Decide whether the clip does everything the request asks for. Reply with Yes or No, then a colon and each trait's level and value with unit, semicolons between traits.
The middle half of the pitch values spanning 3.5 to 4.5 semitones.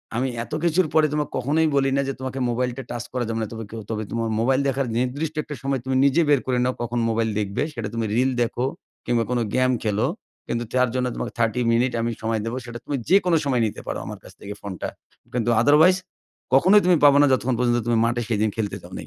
No: average, 3.0 semitones